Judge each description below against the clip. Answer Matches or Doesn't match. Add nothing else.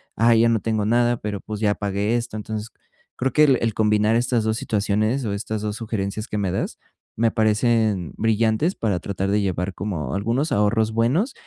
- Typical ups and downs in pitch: Doesn't match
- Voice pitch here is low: Matches